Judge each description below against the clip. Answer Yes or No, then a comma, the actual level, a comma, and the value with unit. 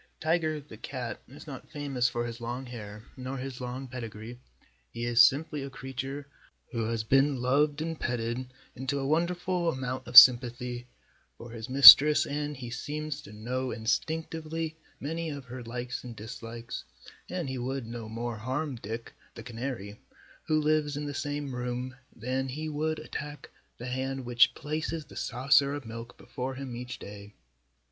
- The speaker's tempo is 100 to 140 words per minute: No, average, 170 wpm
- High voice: No, low, 130 Hz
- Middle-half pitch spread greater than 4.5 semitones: No, average, 3.5 semitones